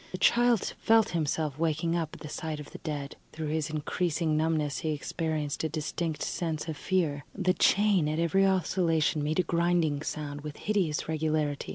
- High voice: No, medium, 160 Hz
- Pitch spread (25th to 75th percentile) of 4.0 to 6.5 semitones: No, narrow, 2.4 semitones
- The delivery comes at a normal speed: Yes, average, 180 wpm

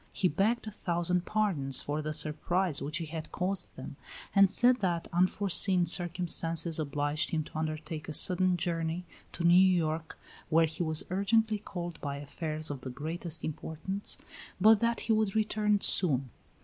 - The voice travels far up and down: No, average, 3.6 semitones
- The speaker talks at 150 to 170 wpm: Yes, average, 160 wpm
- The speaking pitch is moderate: Yes, medium, 170 Hz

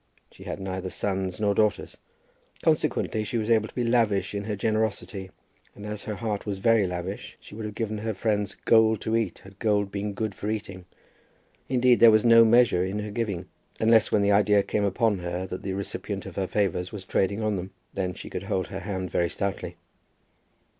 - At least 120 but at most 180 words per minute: No, fast, 205 wpm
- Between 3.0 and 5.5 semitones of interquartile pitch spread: No, narrow, 2.4 semitones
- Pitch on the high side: No, low, 105 Hz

